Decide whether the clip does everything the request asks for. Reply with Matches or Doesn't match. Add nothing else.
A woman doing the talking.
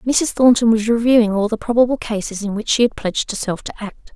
Matches